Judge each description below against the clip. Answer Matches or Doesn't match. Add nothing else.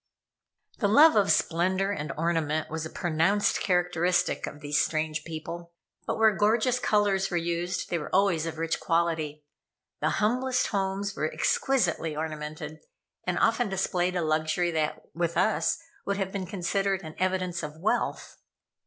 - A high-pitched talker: Doesn't match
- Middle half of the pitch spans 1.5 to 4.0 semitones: Matches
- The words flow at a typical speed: Matches